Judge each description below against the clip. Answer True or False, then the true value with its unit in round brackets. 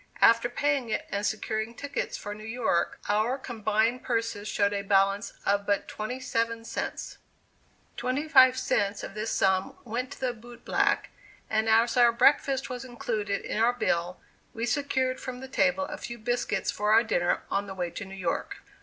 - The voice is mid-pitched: False (225 Hz)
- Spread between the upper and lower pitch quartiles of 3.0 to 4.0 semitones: True (3.4 semitones)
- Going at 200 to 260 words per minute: False (180 wpm)